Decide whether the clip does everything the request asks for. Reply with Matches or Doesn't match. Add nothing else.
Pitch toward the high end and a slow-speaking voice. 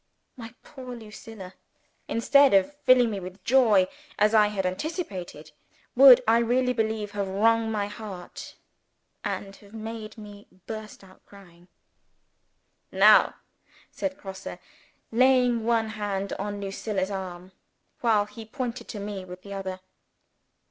Matches